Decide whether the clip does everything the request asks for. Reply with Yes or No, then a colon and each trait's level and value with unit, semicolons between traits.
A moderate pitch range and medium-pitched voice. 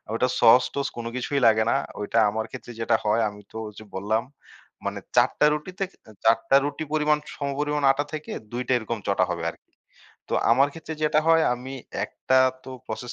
No: average, 4.6 semitones; low, 130 Hz